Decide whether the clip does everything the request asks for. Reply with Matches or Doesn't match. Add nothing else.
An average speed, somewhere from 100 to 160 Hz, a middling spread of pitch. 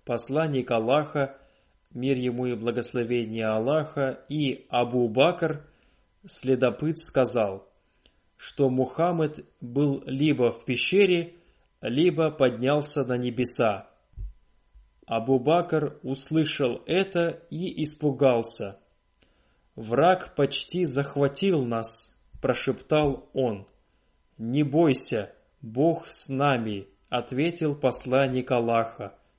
Doesn't match